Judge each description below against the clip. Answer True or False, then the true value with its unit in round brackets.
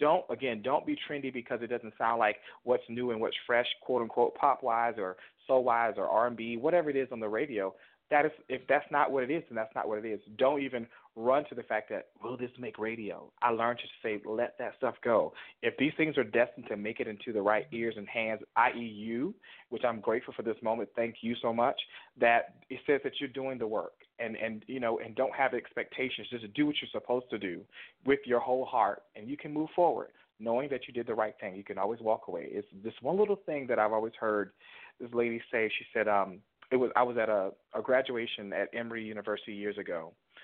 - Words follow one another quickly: True (240 wpm)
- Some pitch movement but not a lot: True (3.0 semitones)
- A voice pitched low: True (120 Hz)